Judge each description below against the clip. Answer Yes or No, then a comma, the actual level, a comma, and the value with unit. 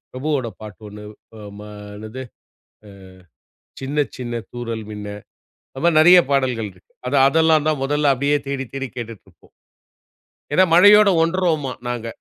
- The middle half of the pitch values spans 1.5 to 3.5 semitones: No, average, 4.9 semitones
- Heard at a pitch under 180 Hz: Yes, low, 135 Hz